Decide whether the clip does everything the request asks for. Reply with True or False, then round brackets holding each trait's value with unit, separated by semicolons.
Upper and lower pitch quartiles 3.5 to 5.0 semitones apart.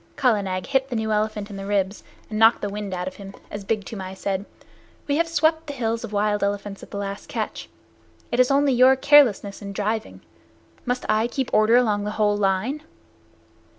True (3.8 semitones)